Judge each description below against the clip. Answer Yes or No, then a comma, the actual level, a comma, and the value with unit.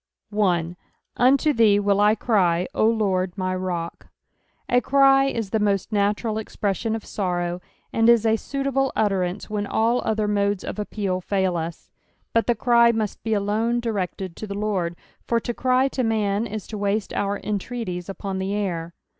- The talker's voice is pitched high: Yes, high, 210 Hz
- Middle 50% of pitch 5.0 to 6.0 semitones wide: No, average, 3.1 semitones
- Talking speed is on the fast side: No, average, 175 wpm